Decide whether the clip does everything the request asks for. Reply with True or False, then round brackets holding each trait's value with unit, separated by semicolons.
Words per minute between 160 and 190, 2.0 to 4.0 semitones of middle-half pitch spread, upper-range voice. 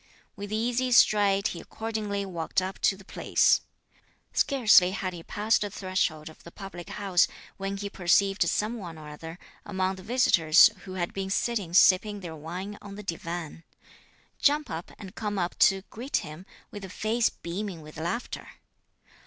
True (170 wpm; 3.2 semitones; 195 Hz)